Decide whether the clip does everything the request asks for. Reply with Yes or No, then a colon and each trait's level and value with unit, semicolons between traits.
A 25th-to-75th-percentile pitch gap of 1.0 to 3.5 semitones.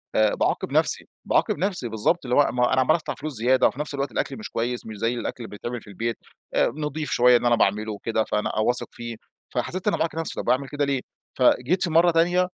No: average, 5.1 semitones